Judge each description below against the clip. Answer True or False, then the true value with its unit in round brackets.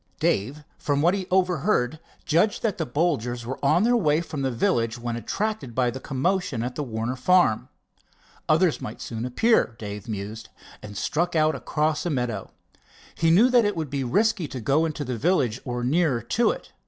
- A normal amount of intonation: False (6.5 semitones)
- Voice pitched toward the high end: False (145 Hz)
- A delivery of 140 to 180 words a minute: False (190 wpm)